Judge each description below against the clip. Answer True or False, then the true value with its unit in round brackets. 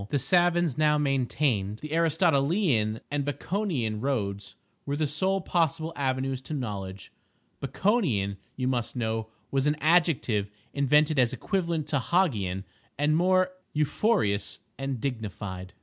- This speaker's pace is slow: True (130 wpm)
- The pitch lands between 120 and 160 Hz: True (140 Hz)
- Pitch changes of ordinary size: False (6.5 semitones)